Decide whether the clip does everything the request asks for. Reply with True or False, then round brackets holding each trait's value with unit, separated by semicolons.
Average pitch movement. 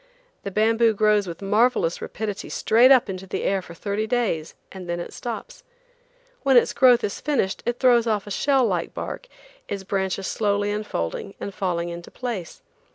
True (3.7 semitones)